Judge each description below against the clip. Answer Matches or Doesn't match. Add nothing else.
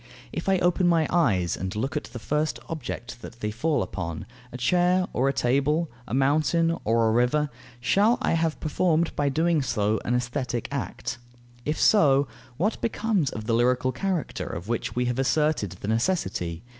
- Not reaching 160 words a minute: Doesn't match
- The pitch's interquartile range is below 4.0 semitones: Doesn't match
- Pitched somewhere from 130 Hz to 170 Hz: Matches